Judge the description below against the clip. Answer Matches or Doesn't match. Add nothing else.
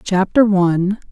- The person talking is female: Matches